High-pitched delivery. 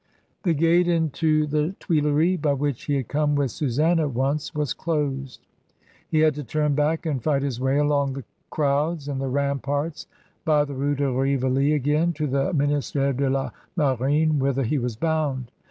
No: medium, 145 Hz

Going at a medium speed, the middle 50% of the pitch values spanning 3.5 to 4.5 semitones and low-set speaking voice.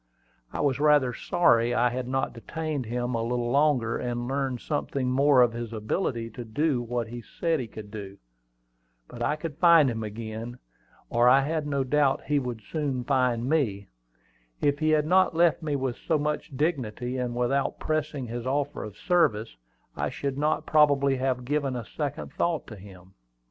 Yes: average, 180 wpm; average, 3.8 semitones; low, 130 Hz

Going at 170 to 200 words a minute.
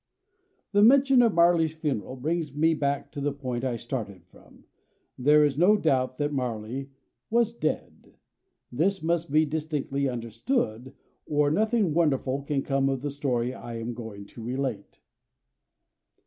No: average, 150 wpm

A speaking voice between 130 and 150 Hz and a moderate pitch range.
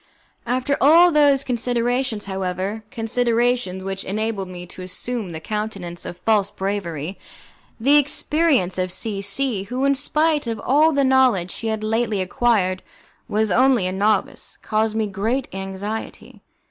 No: high, 220 Hz; average, 4.9 semitones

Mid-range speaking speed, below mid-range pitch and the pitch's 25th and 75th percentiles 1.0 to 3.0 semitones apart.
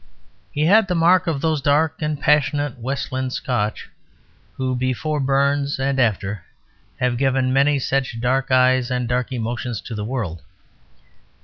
Yes: average, 145 wpm; low, 130 Hz; narrow, 2.6 semitones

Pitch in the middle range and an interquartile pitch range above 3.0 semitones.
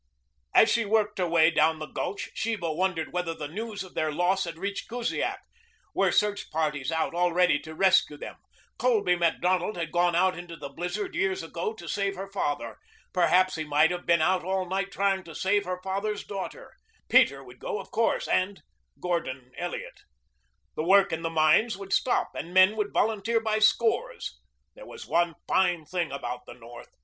Yes: medium, 180 Hz; average, 3.5 semitones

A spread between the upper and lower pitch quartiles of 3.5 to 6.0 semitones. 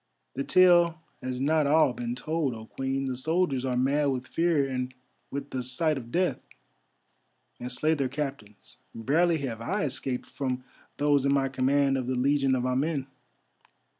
No: average, 2.9 semitones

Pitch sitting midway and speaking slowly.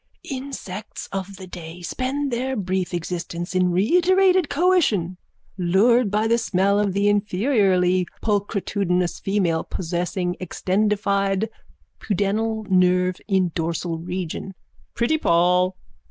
No: high, 195 Hz; slow, 110 wpm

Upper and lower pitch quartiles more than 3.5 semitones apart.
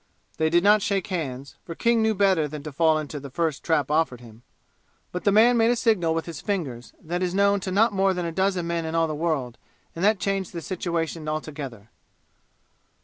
Yes: average, 4.2 semitones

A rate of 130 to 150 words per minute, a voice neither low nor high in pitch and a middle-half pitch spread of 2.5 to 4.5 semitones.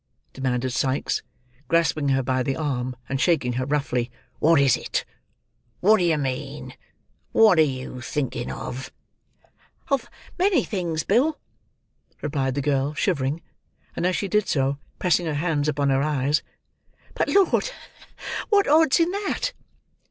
No: average, 145 wpm; medium, 150 Hz; average, 5.3 semitones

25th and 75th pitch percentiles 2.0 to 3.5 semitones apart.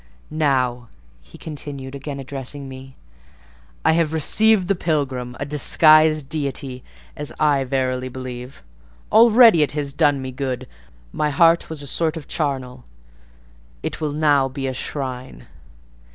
Yes: average, 2.9 semitones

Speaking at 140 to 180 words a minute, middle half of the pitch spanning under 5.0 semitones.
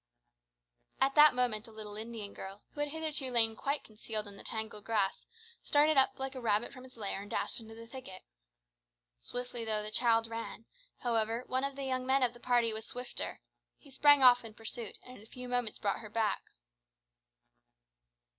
No: average, 195 wpm; average, 3.0 semitones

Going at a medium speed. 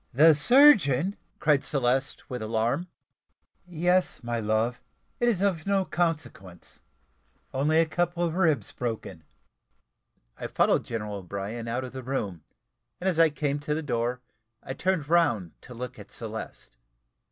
Yes: average, 145 wpm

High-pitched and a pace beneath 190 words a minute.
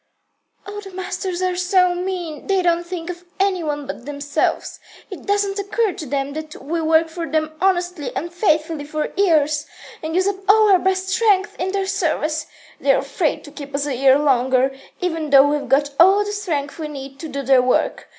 No: very high, 330 Hz; average, 195 wpm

